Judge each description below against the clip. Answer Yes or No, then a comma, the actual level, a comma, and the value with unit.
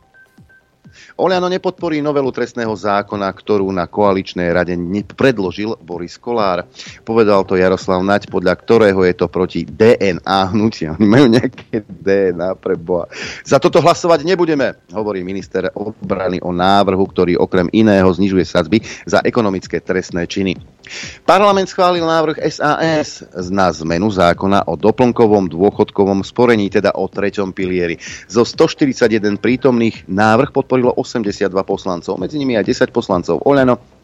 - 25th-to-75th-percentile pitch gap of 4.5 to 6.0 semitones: Yes, average, 5.0 semitones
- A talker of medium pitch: No, low, 100 Hz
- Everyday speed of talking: Yes, average, 130 wpm